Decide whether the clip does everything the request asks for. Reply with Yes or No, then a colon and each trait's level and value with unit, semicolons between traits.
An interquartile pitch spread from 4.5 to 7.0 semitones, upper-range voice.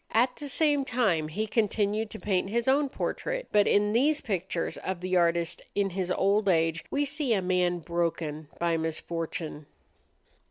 Yes: average, 5.3 semitones; high, 195 Hz